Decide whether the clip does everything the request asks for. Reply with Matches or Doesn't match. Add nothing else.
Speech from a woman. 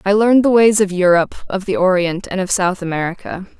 Matches